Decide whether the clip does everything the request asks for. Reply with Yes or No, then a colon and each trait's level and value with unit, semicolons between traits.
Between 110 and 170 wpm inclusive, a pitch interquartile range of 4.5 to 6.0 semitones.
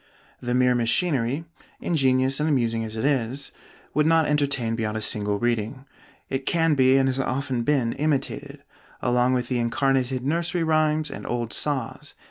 No: average, 160 wpm; average, 3.5 semitones